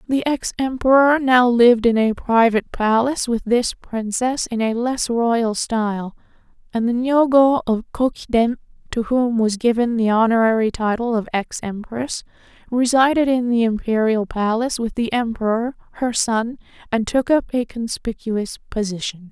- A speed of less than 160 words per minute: Yes, average, 150 wpm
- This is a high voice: Yes, high, 235 Hz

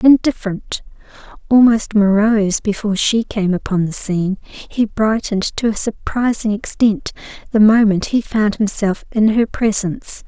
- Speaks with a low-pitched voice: No, high, 210 Hz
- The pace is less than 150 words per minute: Yes, slow, 135 wpm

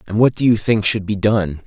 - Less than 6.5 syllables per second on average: Yes, 5.3 syllables/s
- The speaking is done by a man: Yes, male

